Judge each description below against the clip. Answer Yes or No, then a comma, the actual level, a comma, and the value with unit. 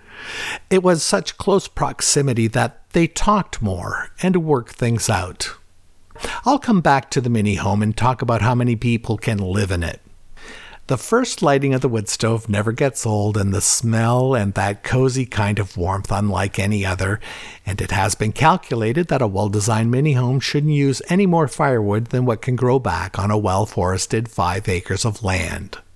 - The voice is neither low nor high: No, low, 115 Hz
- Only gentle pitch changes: No, average, 4.9 semitones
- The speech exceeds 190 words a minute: No, average, 185 wpm